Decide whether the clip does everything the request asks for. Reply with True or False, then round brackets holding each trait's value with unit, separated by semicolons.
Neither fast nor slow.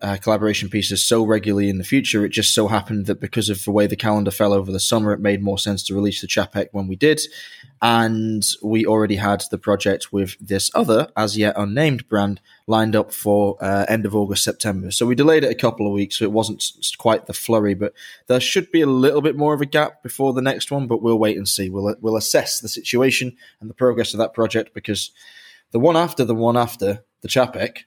False (235 wpm)